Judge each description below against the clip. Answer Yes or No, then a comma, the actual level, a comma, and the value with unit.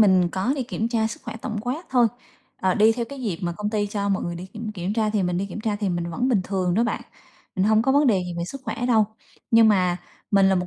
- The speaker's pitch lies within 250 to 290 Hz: No, high, 210 Hz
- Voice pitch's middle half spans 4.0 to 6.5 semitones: No, average, 3.6 semitones